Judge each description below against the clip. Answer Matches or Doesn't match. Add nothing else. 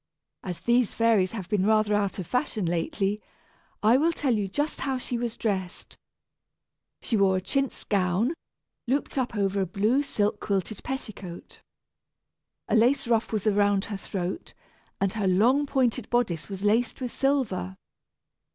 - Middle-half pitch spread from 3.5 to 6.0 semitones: Matches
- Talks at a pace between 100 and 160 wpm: Matches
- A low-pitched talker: Doesn't match